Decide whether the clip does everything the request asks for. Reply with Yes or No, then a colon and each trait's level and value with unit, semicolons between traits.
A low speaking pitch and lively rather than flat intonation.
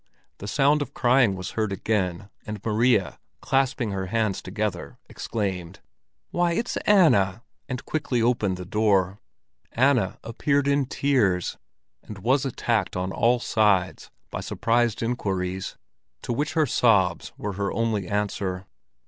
No: low, 110 Hz; average, 4.8 semitones